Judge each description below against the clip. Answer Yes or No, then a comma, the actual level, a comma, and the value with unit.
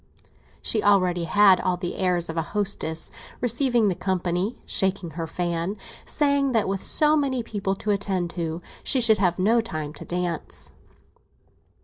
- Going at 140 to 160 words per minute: Yes, average, 155 wpm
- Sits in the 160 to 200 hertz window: Yes, high, 190 Hz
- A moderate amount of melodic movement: Yes, average, 4.0 semitones